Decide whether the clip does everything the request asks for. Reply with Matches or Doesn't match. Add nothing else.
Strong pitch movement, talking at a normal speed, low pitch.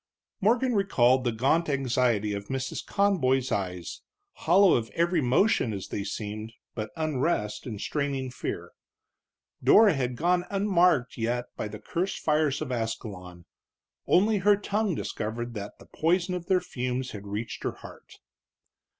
Matches